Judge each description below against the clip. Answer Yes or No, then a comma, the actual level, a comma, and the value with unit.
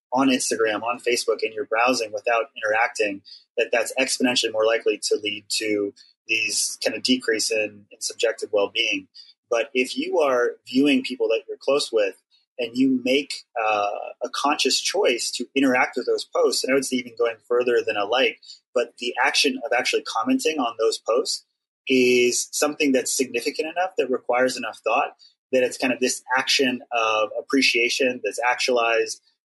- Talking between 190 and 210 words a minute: No, average, 175 wpm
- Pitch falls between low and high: Yes, medium, 150 Hz